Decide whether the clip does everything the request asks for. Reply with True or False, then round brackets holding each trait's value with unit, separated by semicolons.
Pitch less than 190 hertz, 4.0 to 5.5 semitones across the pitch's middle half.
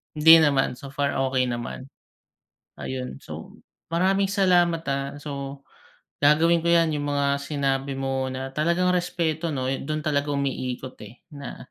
False (140 Hz; 3.4 semitones)